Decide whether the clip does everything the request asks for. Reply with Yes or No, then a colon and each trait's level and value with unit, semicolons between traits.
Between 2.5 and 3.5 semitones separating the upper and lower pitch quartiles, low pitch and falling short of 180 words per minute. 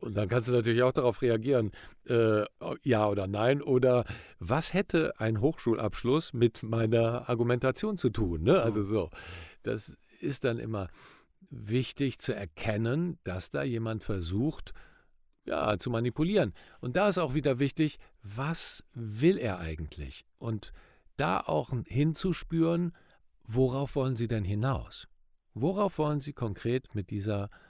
No: average, 4.9 semitones; low, 120 Hz; average, 140 wpm